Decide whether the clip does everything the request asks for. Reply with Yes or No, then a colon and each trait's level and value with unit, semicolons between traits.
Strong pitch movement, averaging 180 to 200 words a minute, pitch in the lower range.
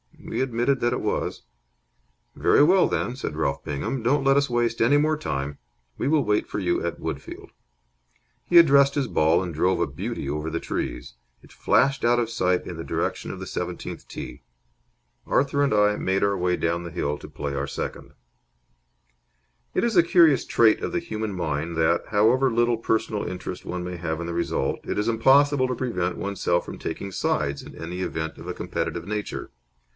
Yes: wide, 7.5 semitones; average, 190 wpm; low, 105 Hz